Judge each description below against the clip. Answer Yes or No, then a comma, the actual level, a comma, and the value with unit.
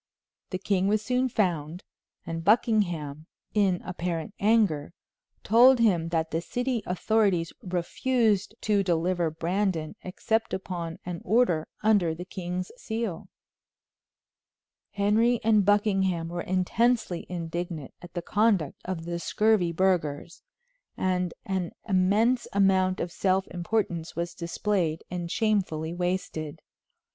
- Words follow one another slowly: Yes, slow, 115 wpm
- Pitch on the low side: No, medium, 185 Hz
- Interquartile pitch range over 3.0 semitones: Yes, average, 3.7 semitones